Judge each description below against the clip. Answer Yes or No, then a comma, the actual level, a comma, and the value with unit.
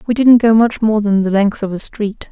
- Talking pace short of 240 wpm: No, fast, 285 wpm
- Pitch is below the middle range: No, high, 215 Hz